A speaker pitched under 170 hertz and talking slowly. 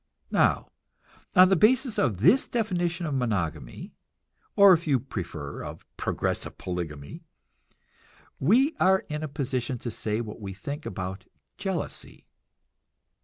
Yes: low, 135 Hz; slow, 120 wpm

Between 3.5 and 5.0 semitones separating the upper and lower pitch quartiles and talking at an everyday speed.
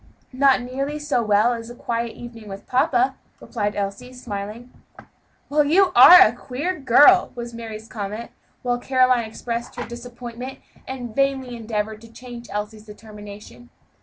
No: average, 2.8 semitones; average, 145 wpm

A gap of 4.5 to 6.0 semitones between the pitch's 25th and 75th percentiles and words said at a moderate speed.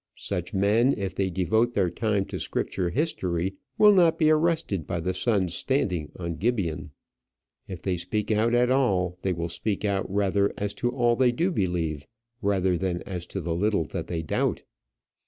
Yes: average, 4.9 semitones; average, 175 wpm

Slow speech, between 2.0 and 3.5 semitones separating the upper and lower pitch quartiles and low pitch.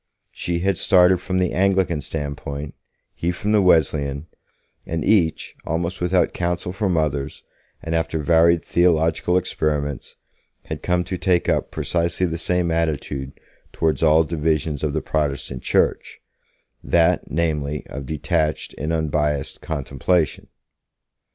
Yes: slow, 130 wpm; average, 2.9 semitones; very low, 80 Hz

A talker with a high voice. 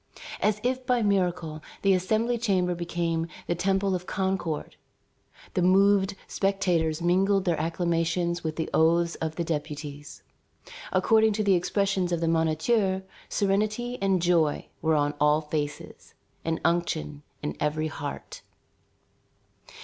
No: medium, 175 Hz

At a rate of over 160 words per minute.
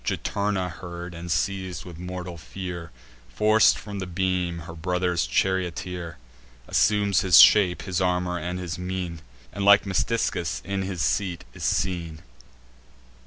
No: slow, 135 wpm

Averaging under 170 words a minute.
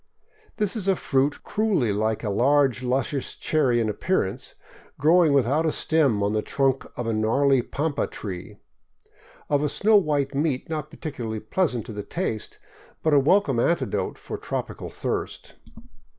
Yes: average, 160 wpm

